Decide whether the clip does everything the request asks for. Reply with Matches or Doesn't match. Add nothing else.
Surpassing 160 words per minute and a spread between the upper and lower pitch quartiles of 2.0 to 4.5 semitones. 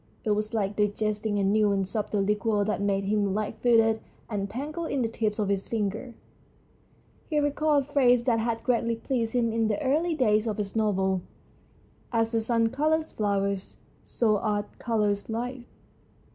Matches